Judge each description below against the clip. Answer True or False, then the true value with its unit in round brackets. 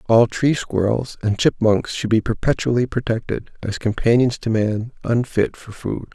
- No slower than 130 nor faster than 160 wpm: True (155 wpm)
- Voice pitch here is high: False (115 Hz)